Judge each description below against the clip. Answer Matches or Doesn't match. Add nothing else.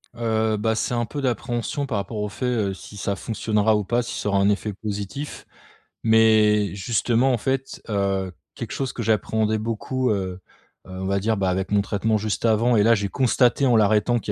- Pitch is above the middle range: Doesn't match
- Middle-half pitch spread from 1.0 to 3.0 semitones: Matches